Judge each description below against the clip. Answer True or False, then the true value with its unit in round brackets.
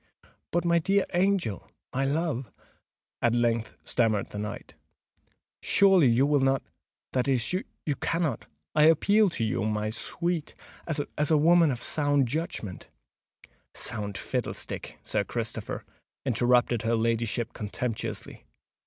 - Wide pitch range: True (6.1 semitones)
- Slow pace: True (115 wpm)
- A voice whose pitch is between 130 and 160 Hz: True (135 Hz)